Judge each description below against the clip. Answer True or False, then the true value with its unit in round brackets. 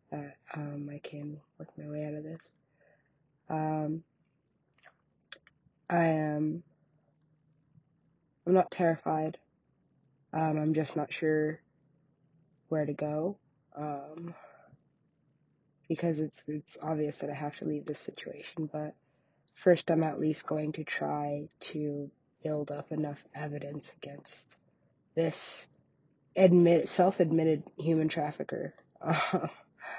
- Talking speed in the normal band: False (110 wpm)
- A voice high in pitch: False (155 Hz)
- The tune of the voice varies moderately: False (1.5 semitones)